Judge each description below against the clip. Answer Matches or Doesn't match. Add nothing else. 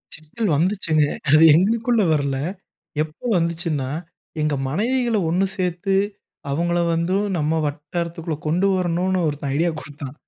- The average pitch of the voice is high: Doesn't match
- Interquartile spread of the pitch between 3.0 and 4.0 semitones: Matches